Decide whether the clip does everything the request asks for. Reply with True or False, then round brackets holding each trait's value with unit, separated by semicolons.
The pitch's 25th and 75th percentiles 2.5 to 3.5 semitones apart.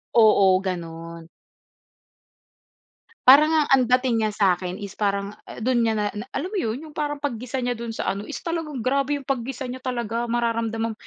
False (4.2 semitones)